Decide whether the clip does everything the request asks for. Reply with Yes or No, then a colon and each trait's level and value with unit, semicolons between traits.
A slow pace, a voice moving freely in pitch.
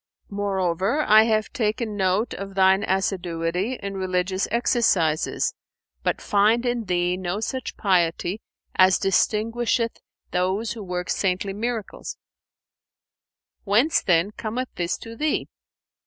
No: slow, 115 wpm; average, 3.7 semitones